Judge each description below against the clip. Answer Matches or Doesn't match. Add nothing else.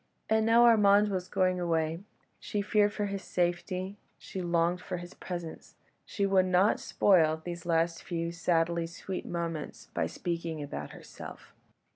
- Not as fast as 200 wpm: Matches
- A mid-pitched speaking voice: Matches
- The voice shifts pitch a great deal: Doesn't match